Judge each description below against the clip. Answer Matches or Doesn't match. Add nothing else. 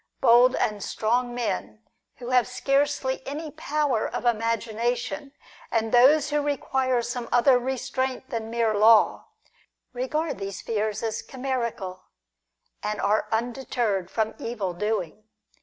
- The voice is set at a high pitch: Matches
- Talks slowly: Matches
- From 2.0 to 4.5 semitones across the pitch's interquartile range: Matches